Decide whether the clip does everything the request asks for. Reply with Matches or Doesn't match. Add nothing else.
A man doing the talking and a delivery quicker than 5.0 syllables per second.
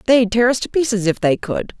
Doesn't match